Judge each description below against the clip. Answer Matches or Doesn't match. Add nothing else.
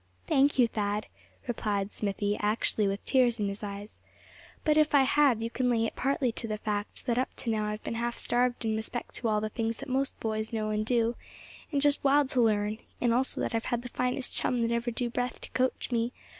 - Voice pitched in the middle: Doesn't match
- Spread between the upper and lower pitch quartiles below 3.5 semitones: Matches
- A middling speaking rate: Doesn't match